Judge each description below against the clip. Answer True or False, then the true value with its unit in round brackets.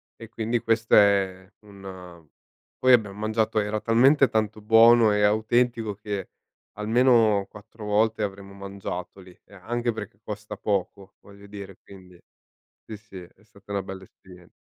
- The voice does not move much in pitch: True (2.3 semitones)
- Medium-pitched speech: False (105 Hz)